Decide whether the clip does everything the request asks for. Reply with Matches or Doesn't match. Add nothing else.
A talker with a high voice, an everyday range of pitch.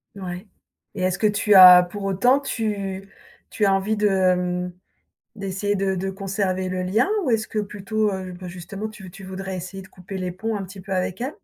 Doesn't match